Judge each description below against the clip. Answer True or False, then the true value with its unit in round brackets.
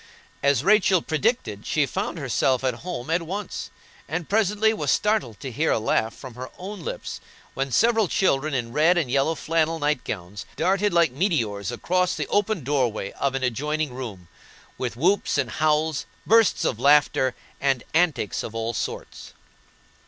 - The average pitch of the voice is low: False (150 Hz)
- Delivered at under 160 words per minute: False (165 wpm)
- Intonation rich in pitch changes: True (6.4 semitones)